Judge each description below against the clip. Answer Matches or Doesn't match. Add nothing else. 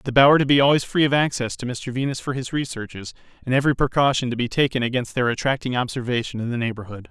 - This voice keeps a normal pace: Doesn't match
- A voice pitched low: Matches